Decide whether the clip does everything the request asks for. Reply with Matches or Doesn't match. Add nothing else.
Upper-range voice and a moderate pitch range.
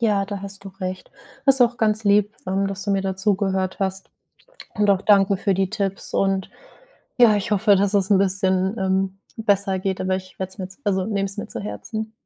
Doesn't match